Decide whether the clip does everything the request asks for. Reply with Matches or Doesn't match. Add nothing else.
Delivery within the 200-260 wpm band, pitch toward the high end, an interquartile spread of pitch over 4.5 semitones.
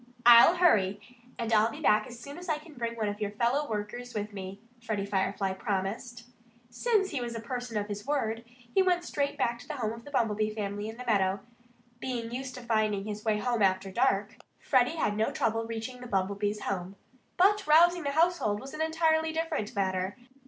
Matches